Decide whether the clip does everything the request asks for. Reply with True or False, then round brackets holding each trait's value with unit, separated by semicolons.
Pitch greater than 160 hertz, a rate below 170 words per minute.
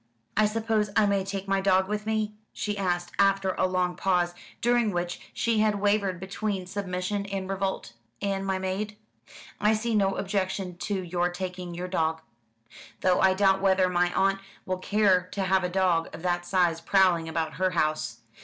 False (190 Hz; 180 wpm)